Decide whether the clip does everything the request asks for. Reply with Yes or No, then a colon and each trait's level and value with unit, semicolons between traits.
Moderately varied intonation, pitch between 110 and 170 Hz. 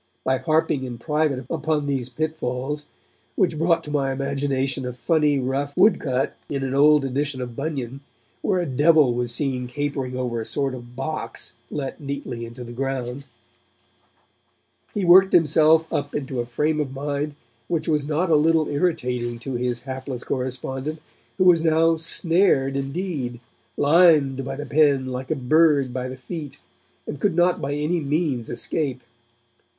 Yes: average, 3.3 semitones; medium, 140 Hz